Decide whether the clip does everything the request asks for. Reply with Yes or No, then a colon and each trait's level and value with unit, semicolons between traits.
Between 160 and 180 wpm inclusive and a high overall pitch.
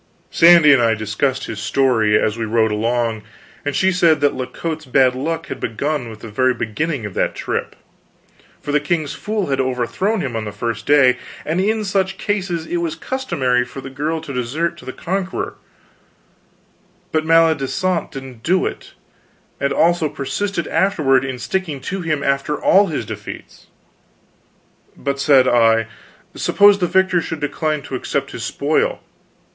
No: average, 165 wpm; medium, 145 Hz